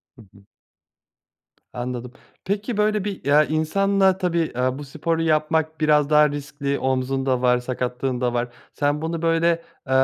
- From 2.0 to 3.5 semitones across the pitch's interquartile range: No, average, 4.2 semitones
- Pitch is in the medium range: Yes, medium, 150 Hz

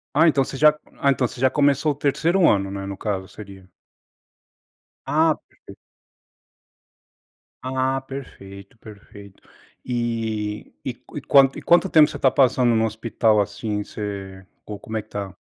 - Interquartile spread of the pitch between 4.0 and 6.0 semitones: Yes, average, 5.1 semitones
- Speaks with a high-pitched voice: No, low, 115 Hz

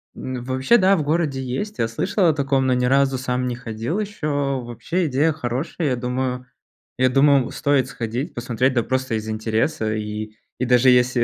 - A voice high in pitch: No, low, 130 Hz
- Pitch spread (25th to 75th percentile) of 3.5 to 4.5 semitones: No, average, 2.8 semitones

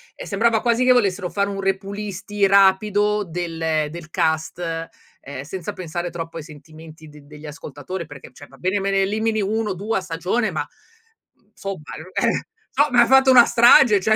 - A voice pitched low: No, high, 190 Hz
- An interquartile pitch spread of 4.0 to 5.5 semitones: Yes, average, 4.4 semitones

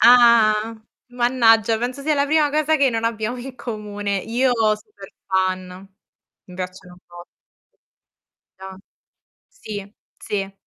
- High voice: Yes, high, 225 Hz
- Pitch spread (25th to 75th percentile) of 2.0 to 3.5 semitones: No, average, 4.1 semitones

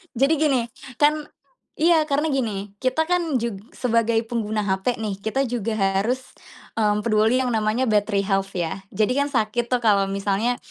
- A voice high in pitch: Yes, high, 230 Hz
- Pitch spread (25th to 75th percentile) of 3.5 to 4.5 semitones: Yes, average, 4.0 semitones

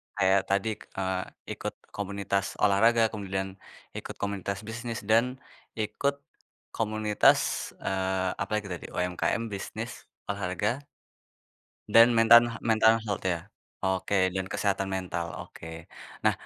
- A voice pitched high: No, low, 100 Hz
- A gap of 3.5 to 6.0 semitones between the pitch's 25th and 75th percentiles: No, average, 2.8 semitones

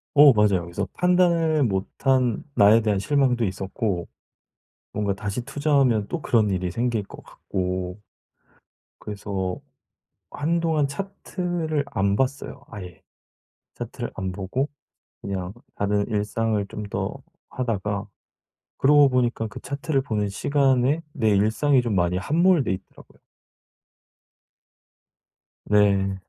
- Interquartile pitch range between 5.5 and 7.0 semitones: Yes, wide, 6.0 semitones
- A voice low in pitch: Yes, low, 110 Hz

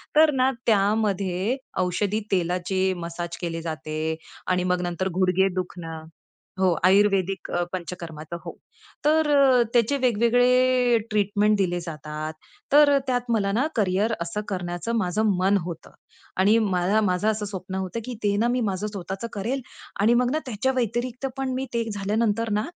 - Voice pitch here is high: Yes, high, 200 Hz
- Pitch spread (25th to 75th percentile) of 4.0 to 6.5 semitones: Yes, average, 4.5 semitones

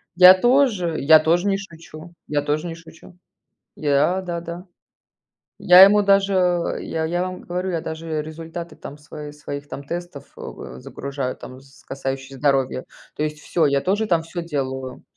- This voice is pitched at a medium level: Yes, medium, 165 Hz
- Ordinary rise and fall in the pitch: Yes, average, 3.7 semitones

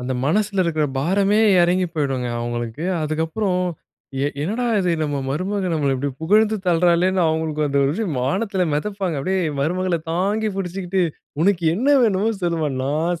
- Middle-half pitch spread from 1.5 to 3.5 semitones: No, average, 4.2 semitones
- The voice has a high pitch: No, medium, 175 Hz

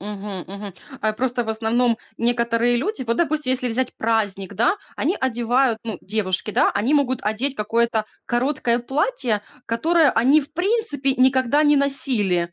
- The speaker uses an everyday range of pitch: Yes, average, 3.9 semitones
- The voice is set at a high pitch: Yes, high, 240 Hz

